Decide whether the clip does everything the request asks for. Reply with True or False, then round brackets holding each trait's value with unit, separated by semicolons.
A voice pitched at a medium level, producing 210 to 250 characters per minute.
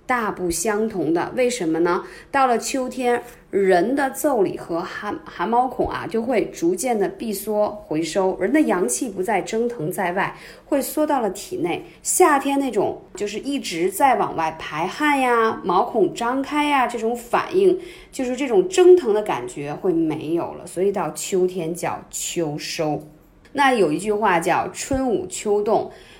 False (250 Hz; 235 characters per minute)